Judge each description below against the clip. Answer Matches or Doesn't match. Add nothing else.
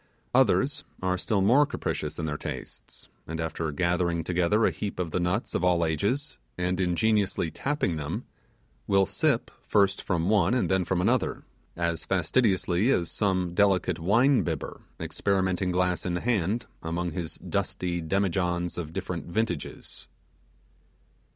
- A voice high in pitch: Doesn't match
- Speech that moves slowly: Doesn't match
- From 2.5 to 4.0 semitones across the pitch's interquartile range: Matches